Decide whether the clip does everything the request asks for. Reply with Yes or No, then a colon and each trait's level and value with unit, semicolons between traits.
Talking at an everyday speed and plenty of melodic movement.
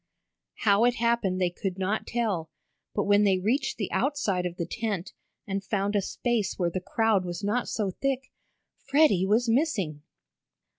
No: average, 165 wpm; average, 4.0 semitones